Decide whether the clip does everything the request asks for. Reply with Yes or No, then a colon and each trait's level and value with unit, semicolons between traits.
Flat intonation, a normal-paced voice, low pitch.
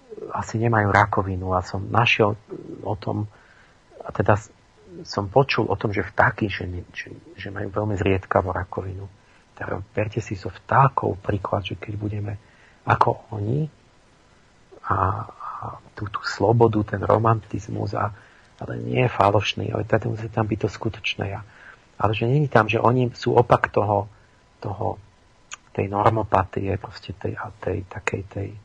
Yes: narrow, 2.2 semitones; average, 150 wpm; low, 105 Hz